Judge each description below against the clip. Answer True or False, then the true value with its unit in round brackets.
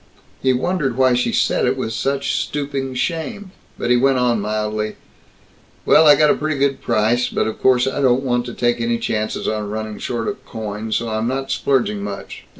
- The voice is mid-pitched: False (125 Hz)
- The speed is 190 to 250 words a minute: True (200 wpm)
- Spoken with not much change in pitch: False (3.7 semitones)